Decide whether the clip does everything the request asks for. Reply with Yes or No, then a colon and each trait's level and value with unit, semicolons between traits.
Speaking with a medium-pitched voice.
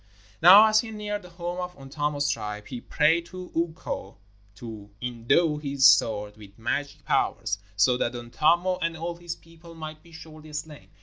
Yes: medium, 155 Hz